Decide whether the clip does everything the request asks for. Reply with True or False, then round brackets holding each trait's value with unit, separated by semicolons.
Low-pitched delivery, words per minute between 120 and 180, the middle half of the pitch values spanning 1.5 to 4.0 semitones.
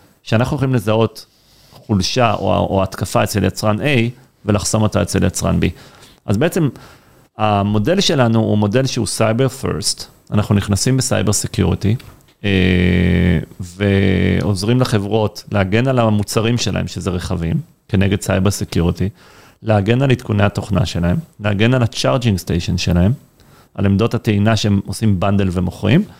True (105 Hz; 130 wpm; 3.4 semitones)